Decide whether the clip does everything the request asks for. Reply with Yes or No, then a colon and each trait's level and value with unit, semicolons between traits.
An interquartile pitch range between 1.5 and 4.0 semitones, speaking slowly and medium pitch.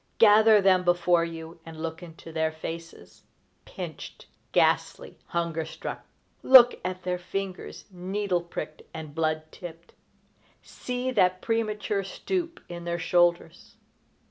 Yes: average, 3.1 semitones; slow, 120 wpm; medium, 175 Hz